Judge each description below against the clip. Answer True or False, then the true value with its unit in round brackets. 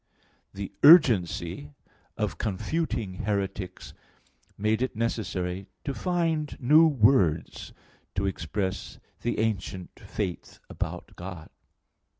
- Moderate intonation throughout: False (6.0 semitones)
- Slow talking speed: True (95 wpm)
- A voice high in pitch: False (105 Hz)